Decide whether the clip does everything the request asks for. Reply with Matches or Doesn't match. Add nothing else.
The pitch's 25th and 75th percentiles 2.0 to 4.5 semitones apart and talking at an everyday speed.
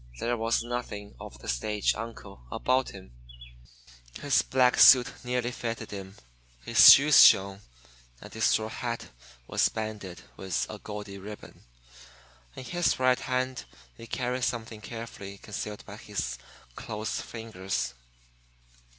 Doesn't match